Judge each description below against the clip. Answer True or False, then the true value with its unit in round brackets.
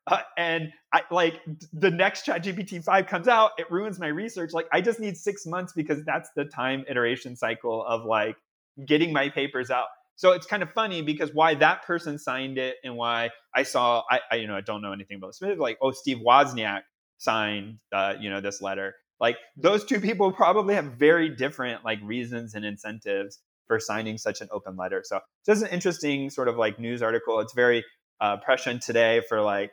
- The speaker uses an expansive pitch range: True (7.1 semitones)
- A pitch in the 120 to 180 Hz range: True (140 Hz)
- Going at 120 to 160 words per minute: False (205 wpm)